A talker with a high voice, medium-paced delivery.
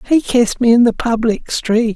No: high, 230 Hz; fast, 215 wpm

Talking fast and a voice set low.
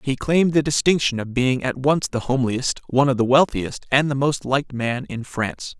Yes: fast, 220 wpm; low, 130 Hz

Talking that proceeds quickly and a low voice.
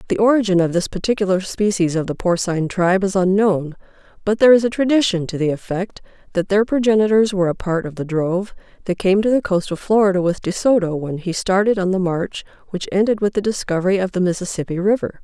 No: fast, 215 wpm; high, 190 Hz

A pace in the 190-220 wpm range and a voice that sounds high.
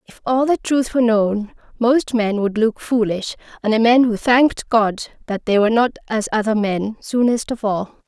Yes: average, 200 wpm; high, 225 Hz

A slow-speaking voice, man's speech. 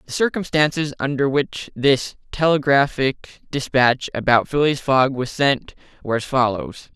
Yes: slow, 130 wpm; male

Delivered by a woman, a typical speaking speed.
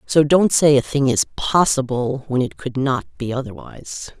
Yes: female; average, 185 wpm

